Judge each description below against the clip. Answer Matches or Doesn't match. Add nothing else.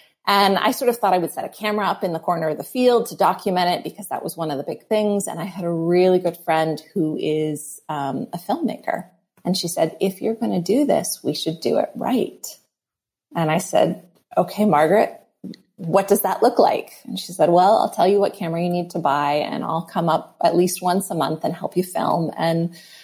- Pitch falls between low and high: Matches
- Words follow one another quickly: Matches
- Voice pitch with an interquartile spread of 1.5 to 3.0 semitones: Doesn't match